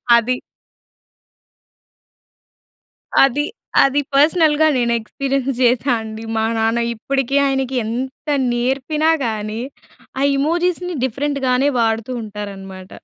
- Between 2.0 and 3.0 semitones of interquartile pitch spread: No, average, 3.8 semitones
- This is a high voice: Yes, very high, 255 Hz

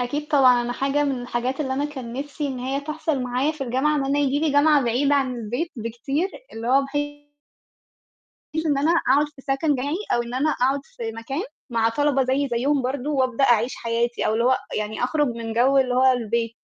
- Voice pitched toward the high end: Yes, very high, 265 Hz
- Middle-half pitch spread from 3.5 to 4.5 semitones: No, average, 3.0 semitones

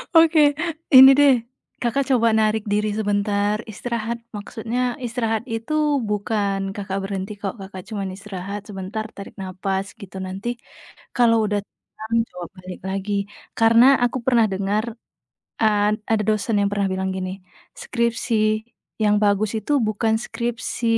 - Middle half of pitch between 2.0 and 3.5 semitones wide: Yes, narrow, 2.6 semitones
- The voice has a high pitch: Yes, high, 210 Hz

